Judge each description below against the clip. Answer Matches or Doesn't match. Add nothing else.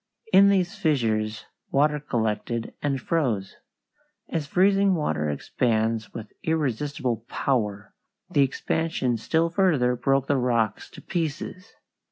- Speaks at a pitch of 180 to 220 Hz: Doesn't match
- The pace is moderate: Doesn't match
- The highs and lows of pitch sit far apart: Matches